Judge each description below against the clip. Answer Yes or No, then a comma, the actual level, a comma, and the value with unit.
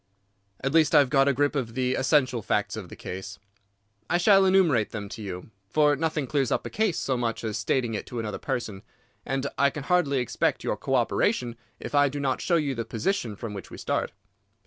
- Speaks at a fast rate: Yes, fast, 220 wpm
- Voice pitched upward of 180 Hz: No, low, 135 Hz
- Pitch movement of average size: Yes, average, 4.4 semitones